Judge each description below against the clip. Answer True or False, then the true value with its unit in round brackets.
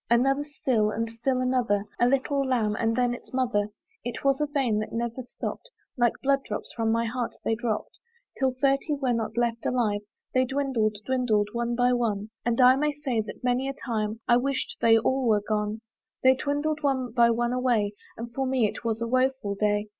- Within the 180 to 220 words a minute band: True (200 wpm)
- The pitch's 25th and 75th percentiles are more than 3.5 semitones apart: False (2.8 semitones)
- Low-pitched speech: False (240 Hz)